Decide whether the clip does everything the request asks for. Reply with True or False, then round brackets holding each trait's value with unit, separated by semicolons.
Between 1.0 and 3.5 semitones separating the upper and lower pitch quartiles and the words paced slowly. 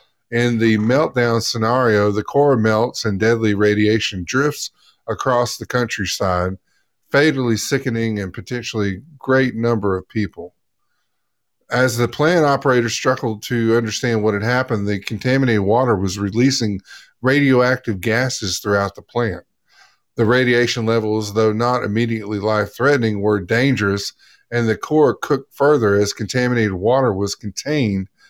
True (3.1 semitones; 130 wpm)